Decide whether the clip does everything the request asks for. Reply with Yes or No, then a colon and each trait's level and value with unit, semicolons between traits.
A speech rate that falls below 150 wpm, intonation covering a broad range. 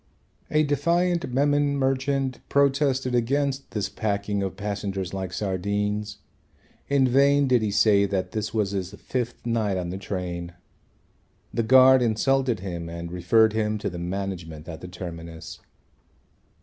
Yes: average, 140 wpm; wide, 5.9 semitones